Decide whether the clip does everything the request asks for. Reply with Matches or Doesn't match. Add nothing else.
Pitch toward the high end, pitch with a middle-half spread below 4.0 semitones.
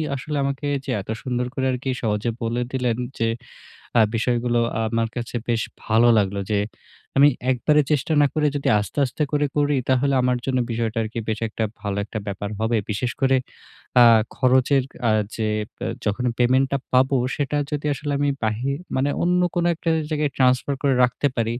Doesn't match